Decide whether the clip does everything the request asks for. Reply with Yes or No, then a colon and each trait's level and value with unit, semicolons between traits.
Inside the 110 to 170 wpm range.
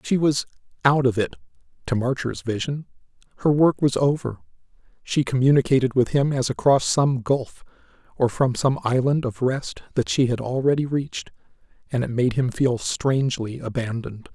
Yes: average, 160 wpm